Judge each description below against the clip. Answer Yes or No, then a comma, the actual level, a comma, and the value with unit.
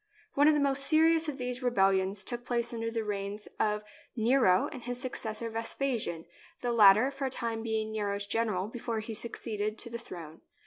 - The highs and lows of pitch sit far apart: No, average, 3.1 semitones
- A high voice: Yes, high, 230 Hz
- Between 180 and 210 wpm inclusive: Yes, average, 190 wpm